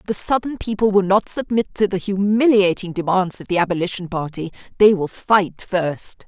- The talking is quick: No, average, 170 wpm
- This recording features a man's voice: No, female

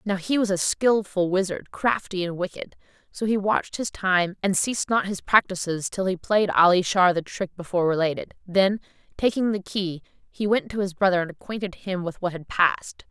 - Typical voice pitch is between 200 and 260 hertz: No, high, 190 Hz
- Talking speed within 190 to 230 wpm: Yes, average, 200 wpm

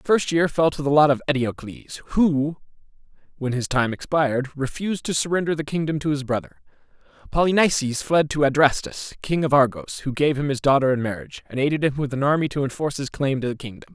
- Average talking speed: No, fast, 210 wpm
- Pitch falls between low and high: Yes, medium, 145 Hz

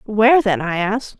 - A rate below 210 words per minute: Yes, average, 200 wpm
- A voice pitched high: Yes, high, 220 Hz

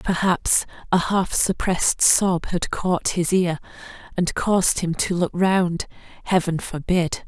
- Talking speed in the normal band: No, slow, 130 wpm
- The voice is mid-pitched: Yes, medium, 180 Hz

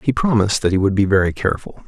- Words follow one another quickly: Yes, fast, 255 wpm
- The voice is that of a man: Yes, male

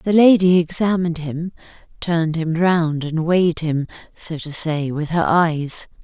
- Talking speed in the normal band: Yes, average, 160 wpm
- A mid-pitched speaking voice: Yes, medium, 165 Hz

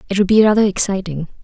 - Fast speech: Yes, fast, 210 wpm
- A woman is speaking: Yes, female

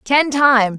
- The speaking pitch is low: No, very high, 255 Hz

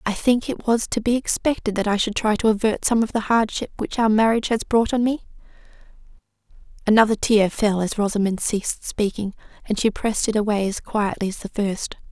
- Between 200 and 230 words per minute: Yes, fast, 205 wpm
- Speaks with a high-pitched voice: Yes, high, 215 Hz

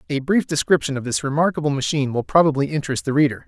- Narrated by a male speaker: Yes, male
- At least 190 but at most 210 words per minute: Yes, fast, 205 wpm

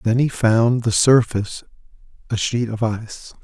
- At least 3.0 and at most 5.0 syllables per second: Yes, 4.6 syllables/s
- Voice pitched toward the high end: No, low, 115 Hz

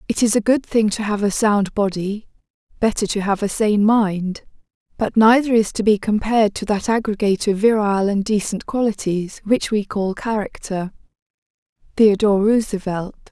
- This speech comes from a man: No, female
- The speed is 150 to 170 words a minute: Yes, average, 160 wpm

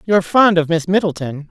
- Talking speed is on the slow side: No, average, 200 wpm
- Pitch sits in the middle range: Yes, medium, 175 Hz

